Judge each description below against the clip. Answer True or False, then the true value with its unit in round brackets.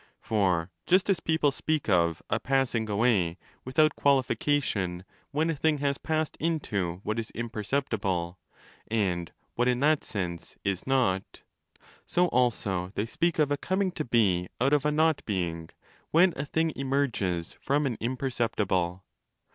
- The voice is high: False (120 Hz)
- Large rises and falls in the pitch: True (7.6 semitones)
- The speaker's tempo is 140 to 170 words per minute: True (155 wpm)